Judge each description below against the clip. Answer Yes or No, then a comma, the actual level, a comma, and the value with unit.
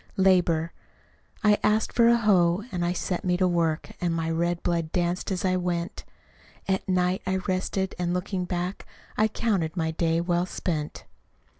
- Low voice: No, medium, 180 Hz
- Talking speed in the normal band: Yes, average, 170 wpm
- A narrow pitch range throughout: Yes, narrow, 1.8 semitones